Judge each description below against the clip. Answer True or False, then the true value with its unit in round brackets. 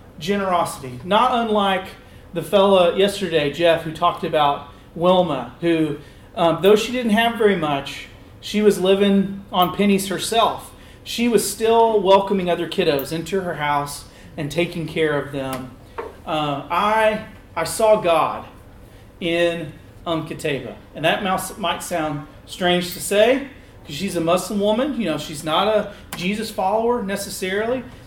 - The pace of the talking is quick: False (145 wpm)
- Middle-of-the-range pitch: True (175 Hz)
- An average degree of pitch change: True (4.8 semitones)